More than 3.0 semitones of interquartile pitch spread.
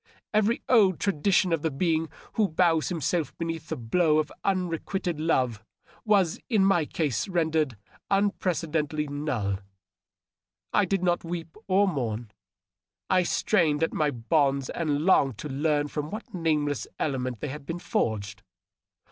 Yes: average, 4.0 semitones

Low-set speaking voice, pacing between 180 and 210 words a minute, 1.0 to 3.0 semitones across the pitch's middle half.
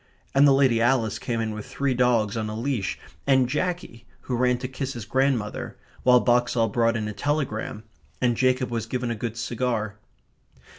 Yes: low, 120 Hz; average, 185 wpm; narrow, 2.5 semitones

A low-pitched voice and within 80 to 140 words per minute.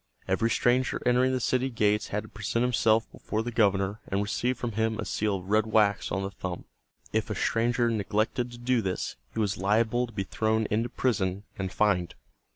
No: low, 110 Hz; average, 200 wpm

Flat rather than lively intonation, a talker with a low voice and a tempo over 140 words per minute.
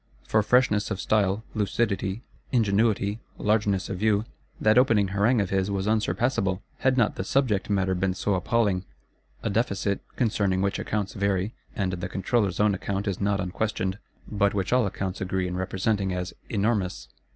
Yes: narrow, 2.2 semitones; low, 100 Hz; average, 160 wpm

